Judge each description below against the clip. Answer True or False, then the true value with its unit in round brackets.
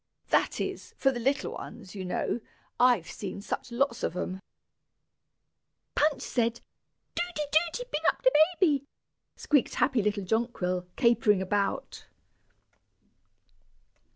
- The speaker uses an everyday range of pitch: False (6.1 semitones)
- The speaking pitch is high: True (235 Hz)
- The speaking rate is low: True (120 wpm)